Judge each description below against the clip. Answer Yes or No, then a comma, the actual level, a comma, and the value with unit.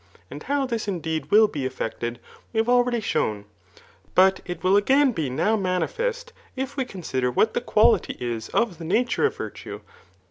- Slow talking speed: No, average, 175 wpm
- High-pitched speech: Yes, high, 205 Hz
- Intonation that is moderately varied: No, wide, 7.7 semitones